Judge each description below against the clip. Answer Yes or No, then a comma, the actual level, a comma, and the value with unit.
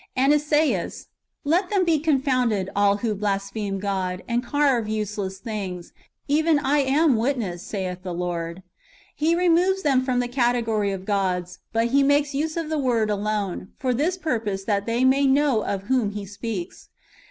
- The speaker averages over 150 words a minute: Yes, average, 170 wpm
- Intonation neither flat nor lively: No, wide, 6.2 semitones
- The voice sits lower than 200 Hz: No, high, 235 Hz